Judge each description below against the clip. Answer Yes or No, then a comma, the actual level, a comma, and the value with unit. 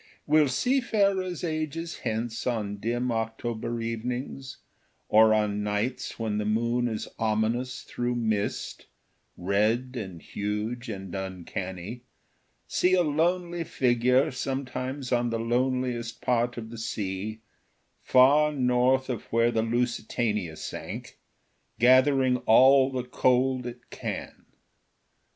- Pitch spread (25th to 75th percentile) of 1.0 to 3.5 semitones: Yes, average, 2.9 semitones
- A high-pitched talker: No, low, 120 Hz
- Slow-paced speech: Yes, slow, 115 wpm